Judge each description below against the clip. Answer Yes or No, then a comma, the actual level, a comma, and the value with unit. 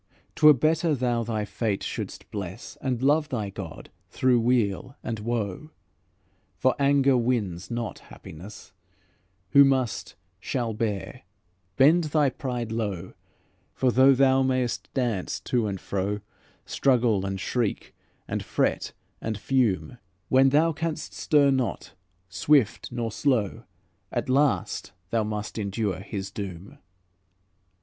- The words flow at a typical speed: No, slow, 125 wpm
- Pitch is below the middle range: Yes, low, 120 Hz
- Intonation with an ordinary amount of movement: Yes, average, 4.5 semitones